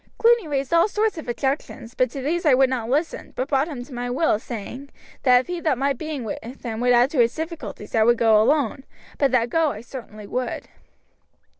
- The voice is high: Yes, very high, 260 Hz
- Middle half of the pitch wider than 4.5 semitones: No, average, 4.0 semitones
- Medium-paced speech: No, fast, 230 wpm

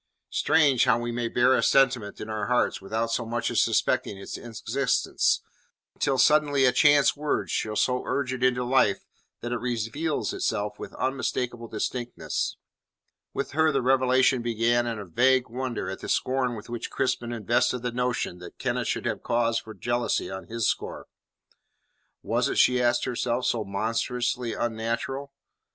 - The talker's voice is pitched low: Yes, low, 120 Hz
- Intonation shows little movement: Yes, narrow, 2.1 semitones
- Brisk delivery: No, average, 165 wpm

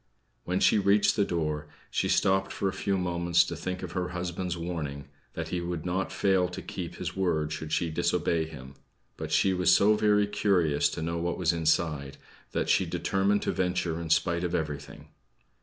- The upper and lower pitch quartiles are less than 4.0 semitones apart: Yes, average, 2.8 semitones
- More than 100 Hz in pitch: No, very low, 85 Hz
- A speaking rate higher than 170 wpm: Yes, average, 190 wpm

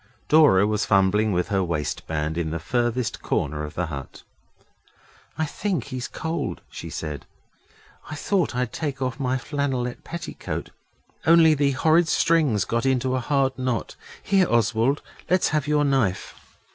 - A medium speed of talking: Yes, average, 150 wpm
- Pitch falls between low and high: No, low, 125 Hz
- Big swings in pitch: Yes, wide, 6.6 semitones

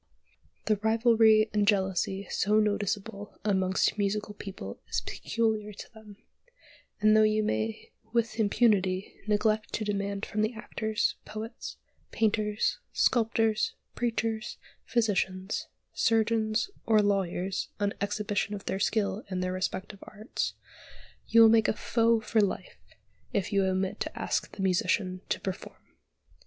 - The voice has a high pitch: Yes, high, 210 Hz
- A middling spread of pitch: No, narrow, 2.0 semitones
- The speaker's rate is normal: No, slow, 130 wpm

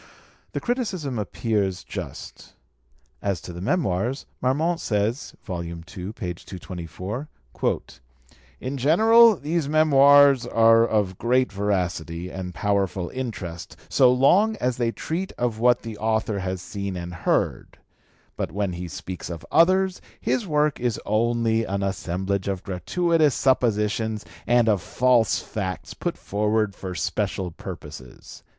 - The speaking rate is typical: No, slow, 125 wpm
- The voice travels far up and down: Yes, wide, 6.0 semitones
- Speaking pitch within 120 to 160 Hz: No, low, 110 Hz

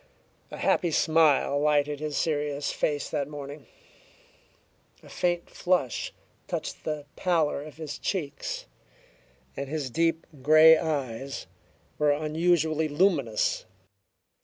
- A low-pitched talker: No, medium, 150 Hz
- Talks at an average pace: No, slow, 110 wpm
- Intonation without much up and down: Yes, narrow, 2.1 semitones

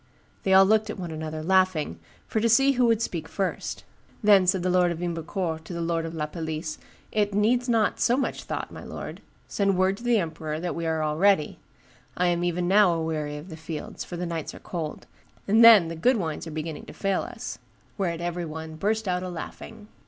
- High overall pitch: No, medium, 175 Hz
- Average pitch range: Yes, average, 3.9 semitones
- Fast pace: Yes, fast, 225 wpm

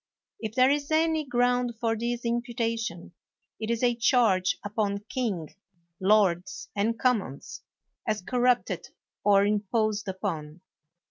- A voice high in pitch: Yes, high, 225 Hz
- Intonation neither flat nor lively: Yes, average, 3.4 semitones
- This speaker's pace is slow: Yes, slow, 120 wpm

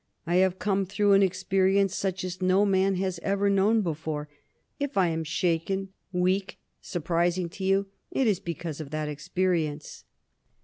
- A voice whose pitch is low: No, medium, 185 Hz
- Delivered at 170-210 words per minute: No, average, 160 wpm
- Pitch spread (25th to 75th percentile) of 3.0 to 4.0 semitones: No, narrow, 2.5 semitones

